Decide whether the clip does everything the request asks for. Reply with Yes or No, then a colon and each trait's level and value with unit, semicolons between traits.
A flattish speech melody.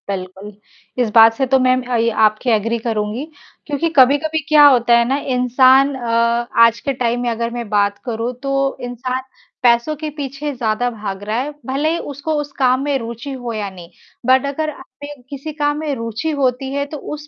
No: average, 3.3 semitones